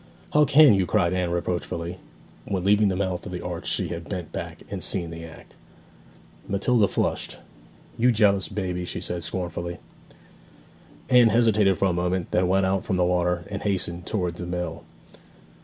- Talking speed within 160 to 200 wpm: Yes, average, 175 wpm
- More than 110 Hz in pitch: No, very low, 90 Hz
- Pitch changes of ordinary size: No, narrow, 2.3 semitones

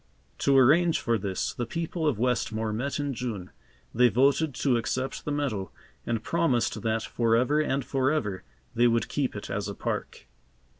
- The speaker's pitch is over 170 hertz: No, low, 125 Hz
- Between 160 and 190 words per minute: Yes, average, 165 wpm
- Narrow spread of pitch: No, average, 4.1 semitones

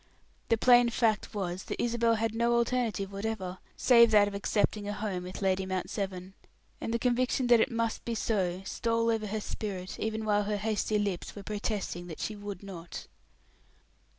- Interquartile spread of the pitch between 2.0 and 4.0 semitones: Yes, average, 2.9 semitones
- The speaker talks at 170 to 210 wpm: Yes, average, 180 wpm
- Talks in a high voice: Yes, high, 210 Hz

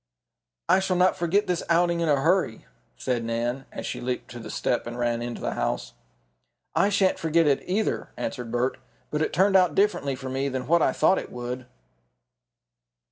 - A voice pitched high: No, medium, 145 Hz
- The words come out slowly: No, average, 190 wpm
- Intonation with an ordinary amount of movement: No, wide, 6.7 semitones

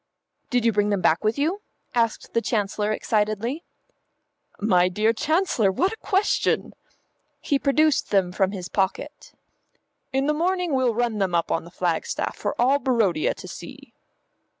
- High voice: Yes, high, 225 Hz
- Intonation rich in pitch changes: Yes, wide, 6.2 semitones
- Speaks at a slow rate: No, average, 155 wpm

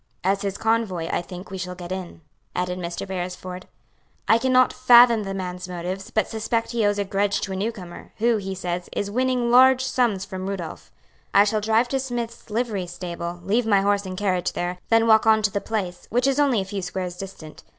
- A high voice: Yes, high, 200 Hz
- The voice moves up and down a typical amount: Yes, average, 3.9 semitones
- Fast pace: Yes, fast, 210 wpm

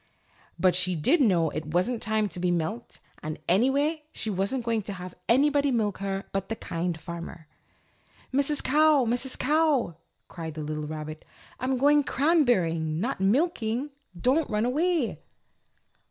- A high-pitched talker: Yes, high, 220 Hz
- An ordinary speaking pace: Yes, average, 150 wpm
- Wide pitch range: Yes, wide, 7.9 semitones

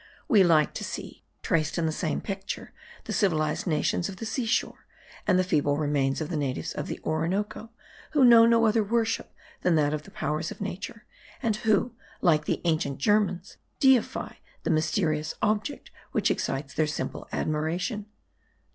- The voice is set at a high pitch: No, medium, 175 Hz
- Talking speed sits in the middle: Yes, average, 170 wpm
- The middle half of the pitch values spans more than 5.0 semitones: Yes, wide, 5.6 semitones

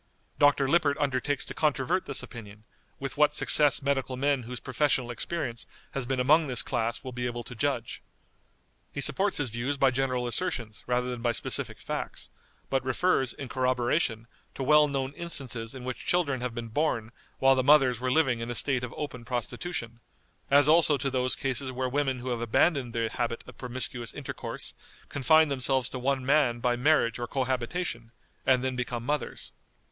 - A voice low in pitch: Yes, low, 130 Hz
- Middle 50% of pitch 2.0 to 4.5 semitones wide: Yes, average, 2.8 semitones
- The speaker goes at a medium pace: Yes, average, 180 wpm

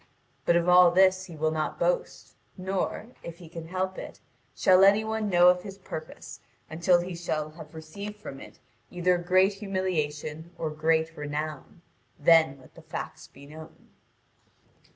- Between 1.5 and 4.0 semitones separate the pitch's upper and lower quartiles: Yes, average, 3.1 semitones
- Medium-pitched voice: Yes, medium, 175 Hz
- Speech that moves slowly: No, average, 160 wpm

